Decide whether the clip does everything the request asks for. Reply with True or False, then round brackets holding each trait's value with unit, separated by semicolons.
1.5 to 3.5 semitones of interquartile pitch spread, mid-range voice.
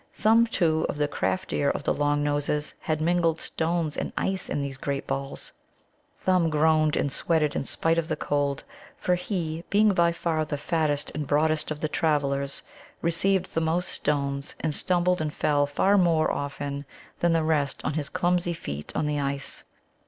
True (2.8 semitones; 155 Hz)